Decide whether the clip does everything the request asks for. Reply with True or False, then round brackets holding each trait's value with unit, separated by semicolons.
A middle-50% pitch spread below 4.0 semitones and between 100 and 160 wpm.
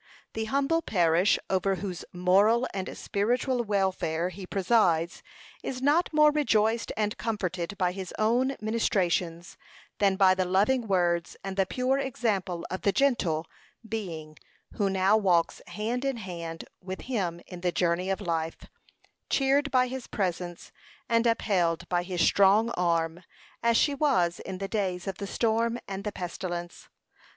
False (4.5 semitones; 150 wpm)